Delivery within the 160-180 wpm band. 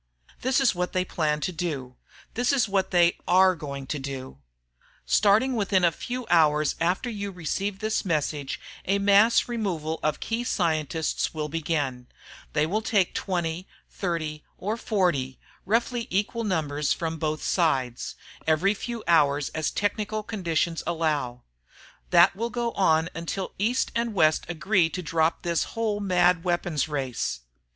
No: average, 150 wpm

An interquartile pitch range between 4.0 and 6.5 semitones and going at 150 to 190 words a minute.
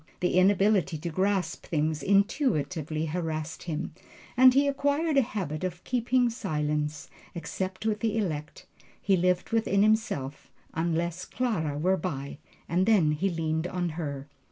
No: average, 5.1 semitones; average, 140 wpm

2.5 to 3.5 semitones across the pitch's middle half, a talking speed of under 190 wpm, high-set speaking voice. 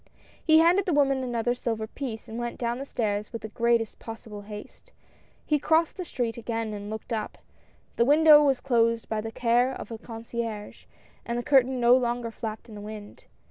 No: average, 2.9 semitones; average, 200 wpm; high, 235 Hz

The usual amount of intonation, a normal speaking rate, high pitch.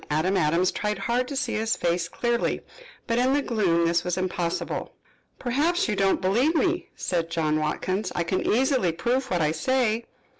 No: wide, 6.7 semitones; average, 185 wpm; high, 195 Hz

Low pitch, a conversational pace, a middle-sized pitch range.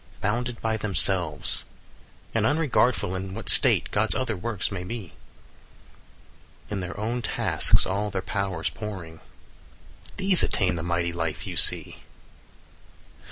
No: low, 100 Hz; slow, 130 wpm; average, 3.9 semitones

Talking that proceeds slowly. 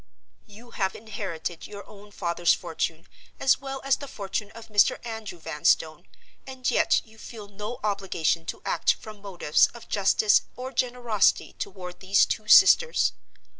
No: average, 150 wpm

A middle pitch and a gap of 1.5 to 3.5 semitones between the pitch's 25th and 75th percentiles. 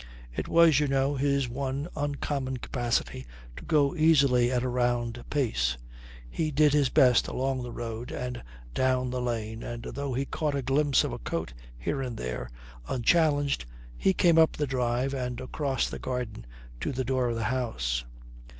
No: low, 130 Hz; average, 2.8 semitones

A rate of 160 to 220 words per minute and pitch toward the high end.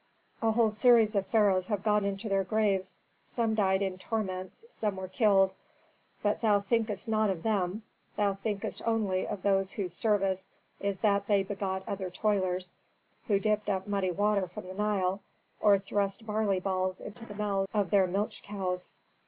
Yes: average, 170 wpm; high, 200 Hz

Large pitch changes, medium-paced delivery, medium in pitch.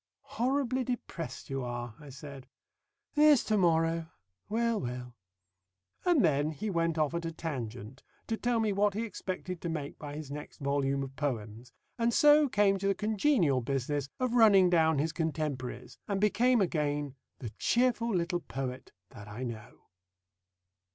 Yes: wide, 7.8 semitones; average, 160 wpm; medium, 165 Hz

